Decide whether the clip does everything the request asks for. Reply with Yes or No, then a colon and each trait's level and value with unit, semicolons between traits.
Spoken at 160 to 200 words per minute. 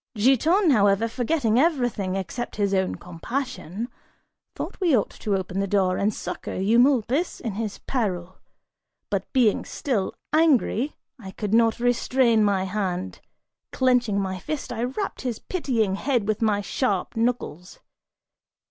No: average, 140 wpm